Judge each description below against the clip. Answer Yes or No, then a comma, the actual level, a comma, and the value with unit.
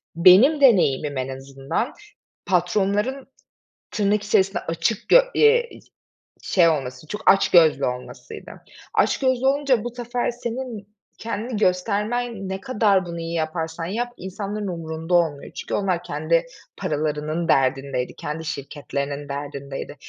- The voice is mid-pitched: Yes, medium, 180 Hz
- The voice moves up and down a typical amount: No, wide, 6.6 semitones